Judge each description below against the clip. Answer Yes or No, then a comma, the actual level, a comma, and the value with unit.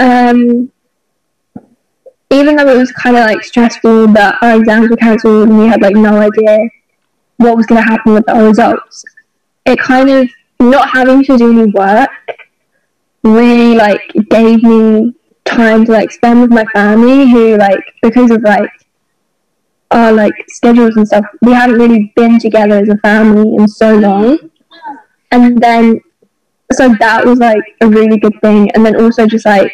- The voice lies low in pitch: No, high, 230 Hz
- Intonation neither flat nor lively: No, narrow, 2.1 semitones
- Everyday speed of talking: Yes, average, 170 wpm